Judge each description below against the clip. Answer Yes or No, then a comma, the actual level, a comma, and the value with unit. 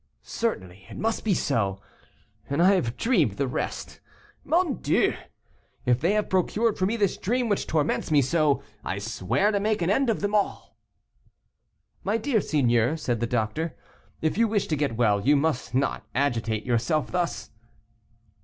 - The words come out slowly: No, average, 170 wpm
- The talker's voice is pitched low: No, medium, 155 Hz